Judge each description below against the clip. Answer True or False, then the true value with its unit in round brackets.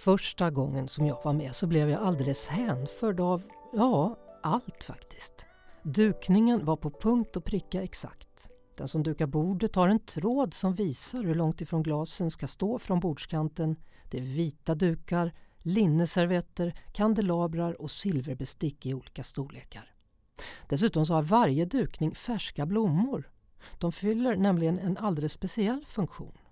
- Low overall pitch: False (170 Hz)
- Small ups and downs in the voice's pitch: False (4.7 semitones)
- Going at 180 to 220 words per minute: False (145 wpm)